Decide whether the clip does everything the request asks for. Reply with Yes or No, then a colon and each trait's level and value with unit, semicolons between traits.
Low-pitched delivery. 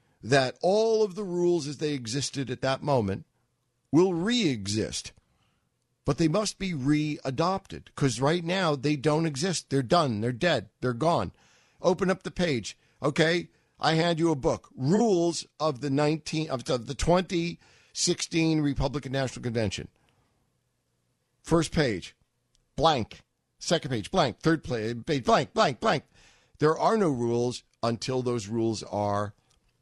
No: medium, 145 Hz